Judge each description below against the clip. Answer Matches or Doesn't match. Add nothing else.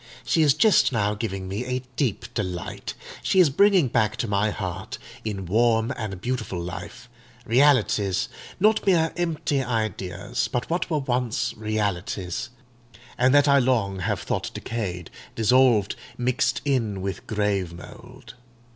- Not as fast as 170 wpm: Matches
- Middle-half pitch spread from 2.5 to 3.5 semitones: Doesn't match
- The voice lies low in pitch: Matches